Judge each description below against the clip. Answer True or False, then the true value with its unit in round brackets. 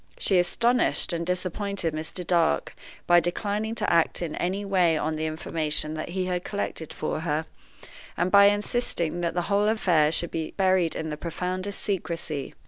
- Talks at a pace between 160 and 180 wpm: True (175 wpm)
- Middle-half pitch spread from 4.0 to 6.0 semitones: False (3.6 semitones)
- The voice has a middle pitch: True (175 Hz)